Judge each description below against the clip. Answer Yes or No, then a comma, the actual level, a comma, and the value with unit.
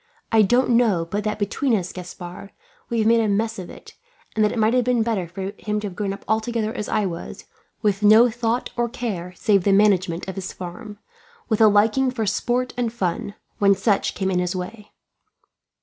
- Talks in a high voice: Yes, high, 210 Hz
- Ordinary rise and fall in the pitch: Yes, average, 3.1 semitones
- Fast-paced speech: Yes, fast, 210 wpm